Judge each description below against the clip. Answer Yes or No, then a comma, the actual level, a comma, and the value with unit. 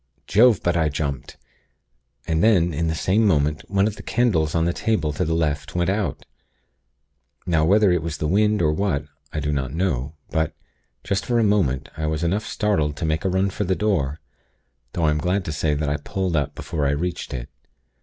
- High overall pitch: No, very low, 80 Hz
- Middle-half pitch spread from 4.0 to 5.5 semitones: Yes, average, 4.4 semitones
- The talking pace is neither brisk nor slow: No, fast, 215 wpm